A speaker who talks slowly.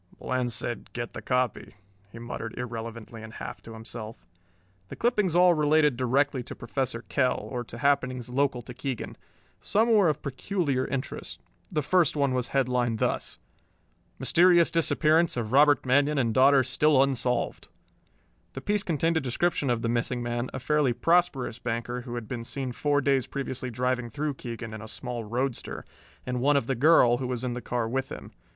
No: average, 180 wpm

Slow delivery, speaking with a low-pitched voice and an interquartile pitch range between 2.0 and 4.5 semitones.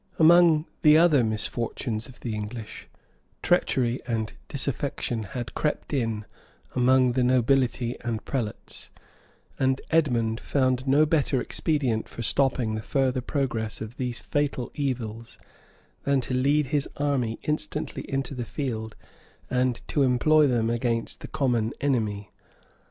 Yes: slow, 130 wpm; low, 125 Hz; average, 3.4 semitones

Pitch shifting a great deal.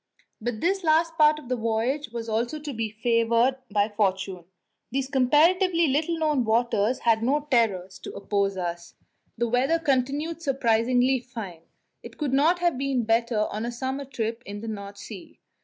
No: average, 4.5 semitones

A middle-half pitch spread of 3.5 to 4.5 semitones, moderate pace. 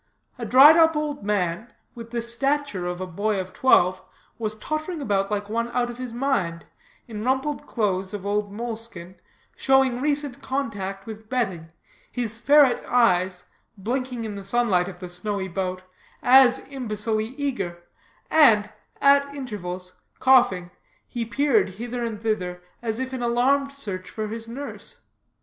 No: average, 5.1 semitones; average, 150 wpm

